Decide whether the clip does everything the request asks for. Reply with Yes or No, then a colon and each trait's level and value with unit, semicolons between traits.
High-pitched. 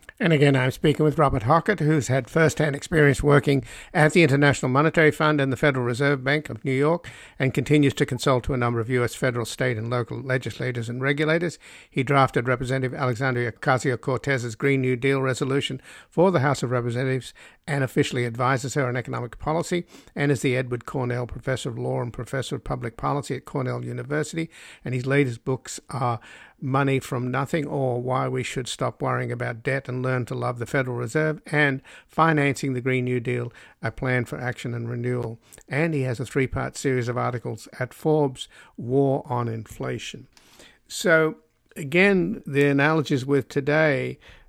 No: low, 135 Hz